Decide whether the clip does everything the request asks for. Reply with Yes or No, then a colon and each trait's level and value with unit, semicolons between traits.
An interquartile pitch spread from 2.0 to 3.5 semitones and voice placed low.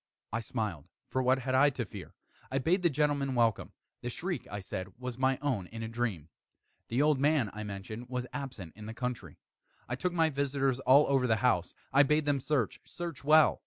No: average, 4.0 semitones; low, 130 Hz